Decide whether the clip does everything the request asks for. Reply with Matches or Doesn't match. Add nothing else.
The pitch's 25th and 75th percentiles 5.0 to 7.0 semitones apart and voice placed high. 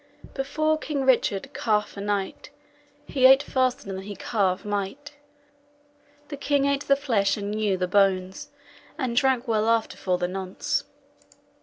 Matches